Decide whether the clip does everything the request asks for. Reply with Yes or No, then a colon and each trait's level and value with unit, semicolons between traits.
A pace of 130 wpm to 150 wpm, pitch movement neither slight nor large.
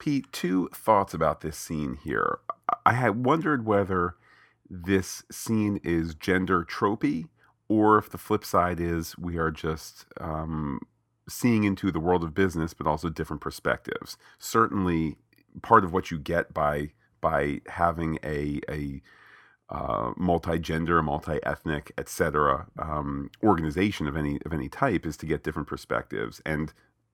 Yes: average, 145 wpm; average, 3.8 semitones